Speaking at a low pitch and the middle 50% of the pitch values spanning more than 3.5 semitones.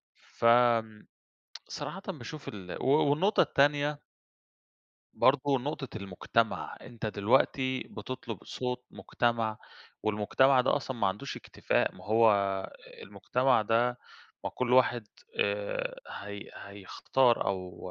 Yes: low, 120 Hz; average, 3.9 semitones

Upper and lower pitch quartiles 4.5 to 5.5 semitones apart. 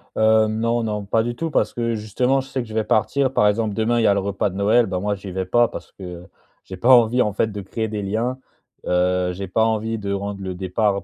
No: average, 2.7 semitones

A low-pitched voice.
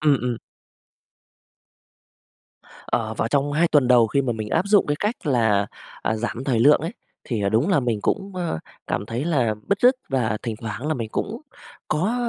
Yes: low, 130 Hz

